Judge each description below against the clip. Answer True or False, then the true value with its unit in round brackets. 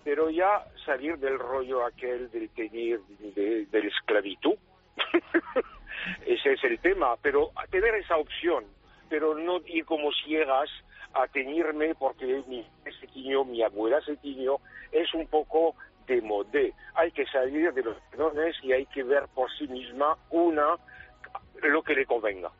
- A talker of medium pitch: True (155 Hz)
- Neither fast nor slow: True (155 wpm)